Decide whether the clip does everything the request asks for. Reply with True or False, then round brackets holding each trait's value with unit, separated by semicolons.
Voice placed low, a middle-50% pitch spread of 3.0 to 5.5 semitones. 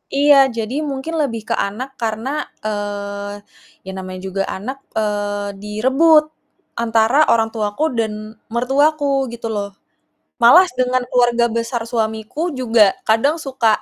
False (230 Hz; 4.2 semitones)